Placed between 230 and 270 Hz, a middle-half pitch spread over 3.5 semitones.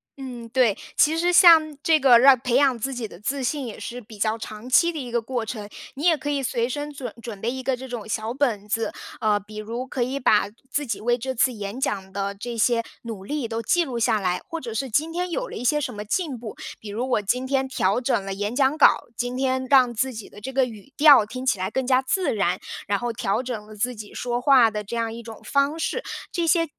Yes: high, 245 Hz; average, 3.9 semitones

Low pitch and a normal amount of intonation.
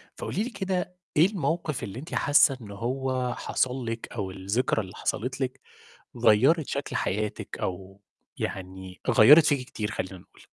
No: low, 125 Hz; wide, 6.3 semitones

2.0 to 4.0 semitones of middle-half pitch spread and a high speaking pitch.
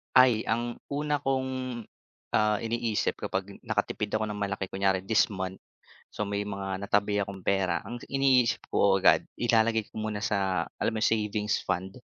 No: average, 3.2 semitones; low, 105 Hz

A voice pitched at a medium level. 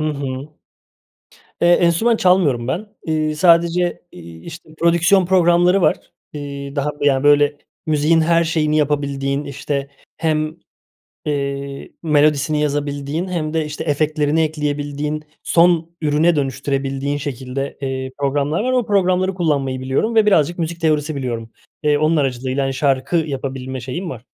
Yes: medium, 150 Hz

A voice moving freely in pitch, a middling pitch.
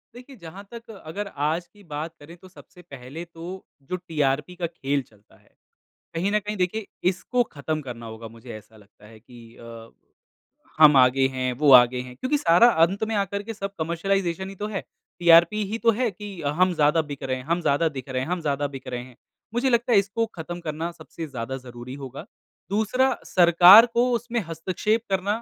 Yes: wide, 6.7 semitones; medium, 165 Hz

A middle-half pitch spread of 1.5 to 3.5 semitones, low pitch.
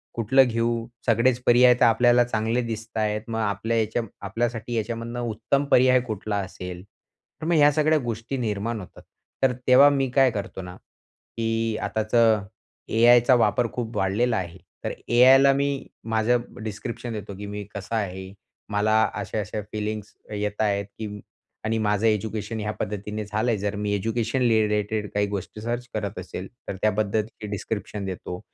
Yes: narrow, 2.4 semitones; low, 110 Hz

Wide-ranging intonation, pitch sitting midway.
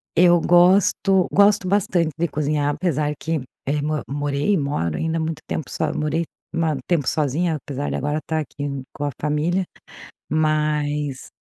No: average, 2.7 semitones; medium, 155 Hz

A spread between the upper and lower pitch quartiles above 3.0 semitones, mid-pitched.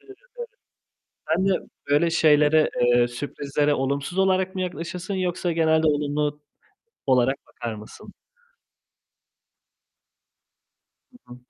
Yes: average, 4.0 semitones; medium, 150 Hz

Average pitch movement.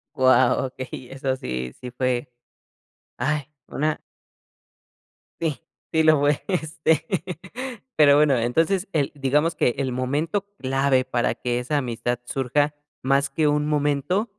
Yes: average, 3.0 semitones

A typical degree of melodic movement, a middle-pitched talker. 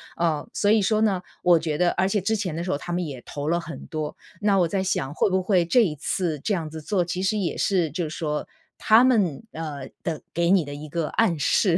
Yes: average, 3.9 semitones; medium, 175 Hz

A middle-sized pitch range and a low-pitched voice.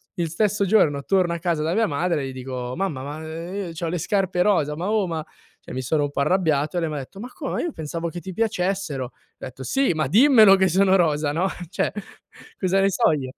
No: average, 4.6 semitones; medium, 170 Hz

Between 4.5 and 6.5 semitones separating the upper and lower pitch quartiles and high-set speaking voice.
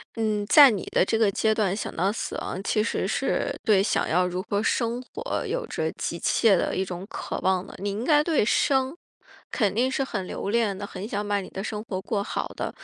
No: average, 3.4 semitones; high, 210 Hz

